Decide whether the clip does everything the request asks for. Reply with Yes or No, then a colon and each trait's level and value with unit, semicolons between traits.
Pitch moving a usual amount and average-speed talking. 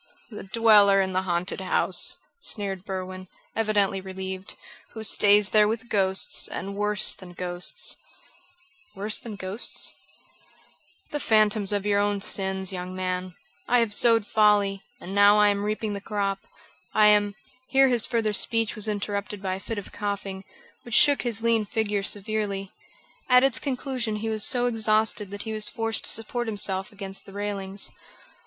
No: narrow, 2.1 semitones; average, 165 wpm